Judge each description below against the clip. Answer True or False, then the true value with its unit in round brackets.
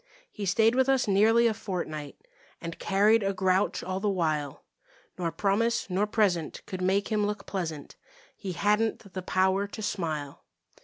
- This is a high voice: True (195 Hz)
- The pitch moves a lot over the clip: False (2.8 semitones)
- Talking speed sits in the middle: True (160 wpm)